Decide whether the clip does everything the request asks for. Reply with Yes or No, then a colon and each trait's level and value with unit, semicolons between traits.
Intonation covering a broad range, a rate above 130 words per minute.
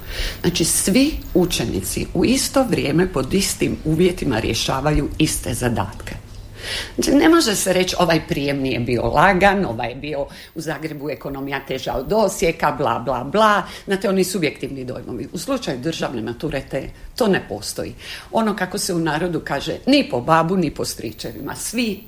Yes: wide, 6.4 semitones; fast, 160 wpm